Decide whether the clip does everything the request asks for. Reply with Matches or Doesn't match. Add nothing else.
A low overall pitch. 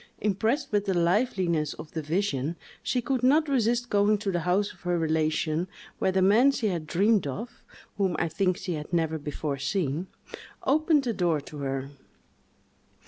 Doesn't match